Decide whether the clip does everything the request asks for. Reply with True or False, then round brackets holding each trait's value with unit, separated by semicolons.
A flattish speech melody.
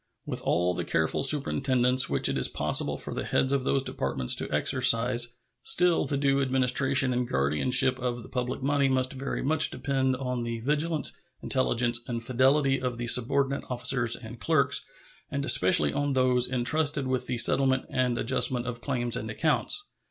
True (2.3 semitones)